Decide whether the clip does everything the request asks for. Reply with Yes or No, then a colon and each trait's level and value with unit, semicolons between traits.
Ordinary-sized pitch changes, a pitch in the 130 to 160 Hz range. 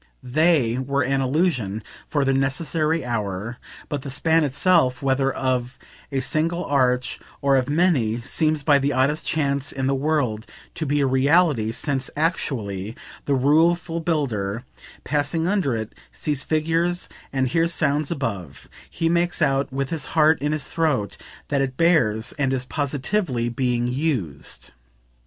Yes: average, 3.9 semitones; medium, 140 Hz